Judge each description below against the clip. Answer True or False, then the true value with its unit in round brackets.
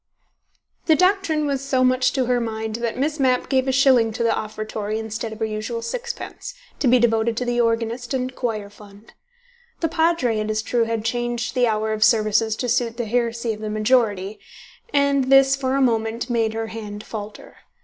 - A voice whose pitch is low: False (235 Hz)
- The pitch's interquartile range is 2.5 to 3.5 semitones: True (2.9 semitones)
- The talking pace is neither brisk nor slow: True (195 wpm)